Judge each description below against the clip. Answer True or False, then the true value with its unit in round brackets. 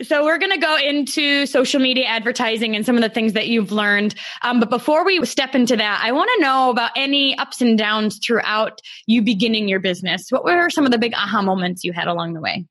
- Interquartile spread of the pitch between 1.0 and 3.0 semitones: False (4.4 semitones)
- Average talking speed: False (240 wpm)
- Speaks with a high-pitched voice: True (235 Hz)